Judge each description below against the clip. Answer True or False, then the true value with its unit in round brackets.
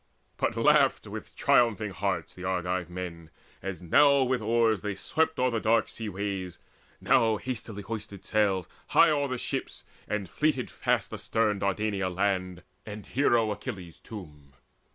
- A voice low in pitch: True (105 Hz)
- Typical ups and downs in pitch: True (3.7 semitones)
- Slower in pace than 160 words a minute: True (150 wpm)